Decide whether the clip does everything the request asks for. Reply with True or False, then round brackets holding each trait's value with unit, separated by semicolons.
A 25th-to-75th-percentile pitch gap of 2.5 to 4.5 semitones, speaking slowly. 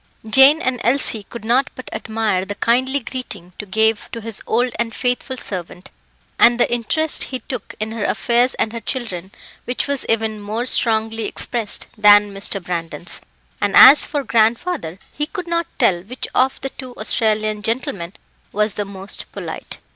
False (3.6 semitones; 170 wpm)